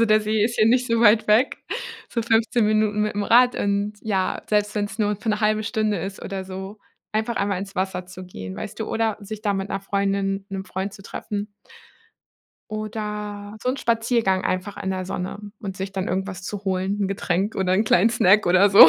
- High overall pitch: Yes, high, 205 Hz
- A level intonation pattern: Yes, narrow, 2.0 semitones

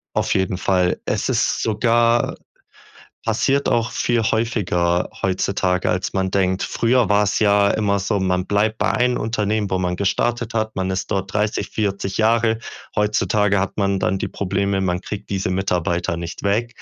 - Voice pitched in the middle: No, low, 100 Hz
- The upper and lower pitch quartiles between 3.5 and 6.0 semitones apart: No, average, 2.7 semitones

